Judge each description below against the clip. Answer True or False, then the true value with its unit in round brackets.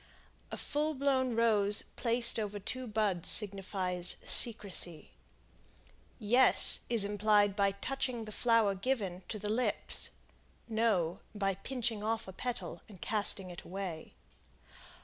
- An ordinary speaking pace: False (125 wpm)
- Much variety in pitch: False (3.1 semitones)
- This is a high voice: True (210 Hz)